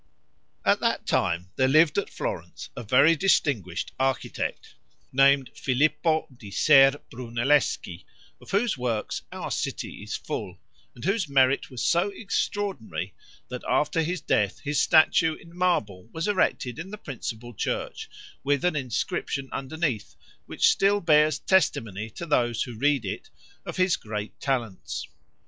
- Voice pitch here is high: No, medium, 140 Hz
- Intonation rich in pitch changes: Yes, wide, 5.9 semitones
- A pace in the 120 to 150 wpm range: Yes, average, 140 wpm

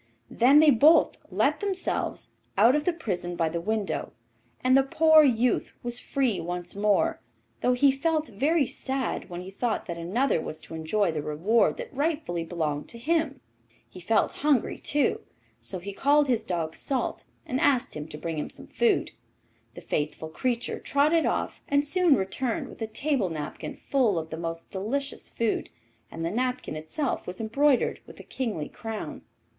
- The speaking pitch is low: No, high, 230 Hz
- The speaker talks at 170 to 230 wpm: Yes, average, 175 wpm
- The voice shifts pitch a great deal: Yes, wide, 8.3 semitones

